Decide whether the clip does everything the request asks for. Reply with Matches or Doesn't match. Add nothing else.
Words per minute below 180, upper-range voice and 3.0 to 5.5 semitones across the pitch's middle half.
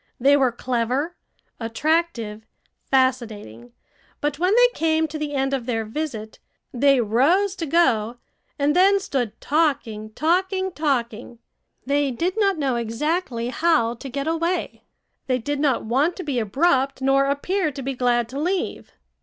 Matches